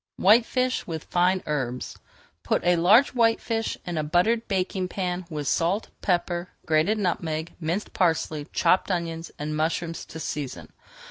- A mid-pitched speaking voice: Yes, medium, 175 Hz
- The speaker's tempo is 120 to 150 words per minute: Yes, average, 140 wpm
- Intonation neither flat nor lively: Yes, average, 3.3 semitones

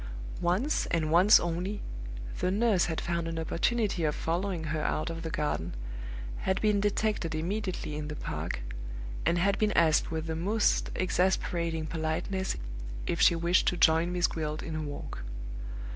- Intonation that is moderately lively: Yes, average, 3.0 semitones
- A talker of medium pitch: Yes, medium, 170 Hz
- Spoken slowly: No, average, 160 wpm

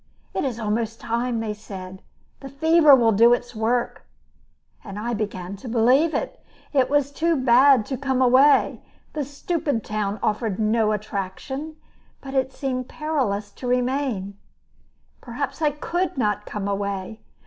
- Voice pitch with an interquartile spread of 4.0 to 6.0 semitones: Yes, average, 4.5 semitones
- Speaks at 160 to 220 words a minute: No, average, 150 wpm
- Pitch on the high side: Yes, high, 240 Hz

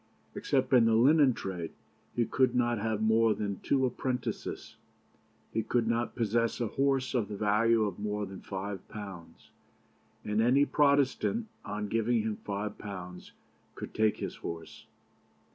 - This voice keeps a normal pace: Yes, average, 150 wpm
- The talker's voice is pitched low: Yes, low, 110 Hz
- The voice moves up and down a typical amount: Yes, average, 3.0 semitones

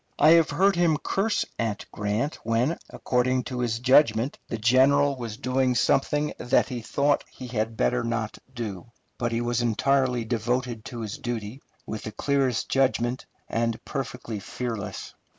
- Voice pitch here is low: Yes, low, 125 Hz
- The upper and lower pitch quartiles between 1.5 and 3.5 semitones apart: Yes, average, 2.9 semitones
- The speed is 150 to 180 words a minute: Yes, average, 155 wpm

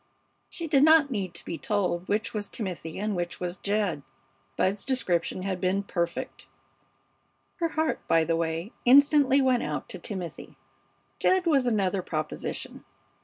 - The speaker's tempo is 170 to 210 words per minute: No, average, 150 wpm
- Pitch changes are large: Yes, wide, 7.0 semitones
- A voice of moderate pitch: No, high, 200 Hz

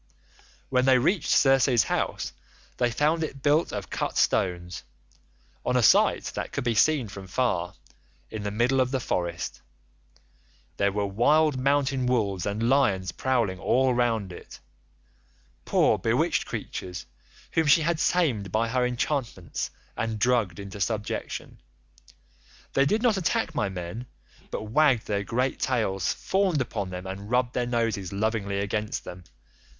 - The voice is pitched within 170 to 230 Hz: No, low, 115 Hz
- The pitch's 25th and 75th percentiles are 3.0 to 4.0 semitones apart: No, average, 5.2 semitones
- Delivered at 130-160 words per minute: Yes, average, 145 wpm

